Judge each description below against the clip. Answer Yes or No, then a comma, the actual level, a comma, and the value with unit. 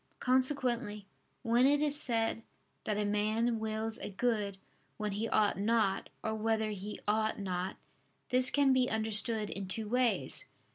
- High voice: Yes, high, 220 Hz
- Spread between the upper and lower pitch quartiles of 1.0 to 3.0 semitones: Yes, narrow, 2.6 semitones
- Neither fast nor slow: Yes, average, 150 wpm